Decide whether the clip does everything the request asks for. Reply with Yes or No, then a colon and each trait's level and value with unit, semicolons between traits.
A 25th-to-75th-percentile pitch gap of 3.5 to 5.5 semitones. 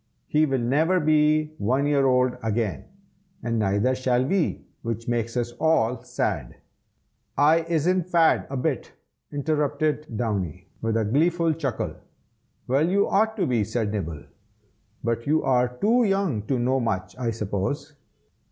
Yes: average, 5.2 semitones